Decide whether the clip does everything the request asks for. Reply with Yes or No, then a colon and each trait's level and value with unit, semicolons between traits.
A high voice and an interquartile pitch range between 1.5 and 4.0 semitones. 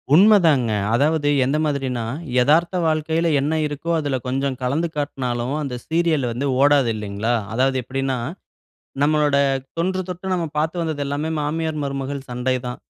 No: medium, 145 Hz; average, 3.4 semitones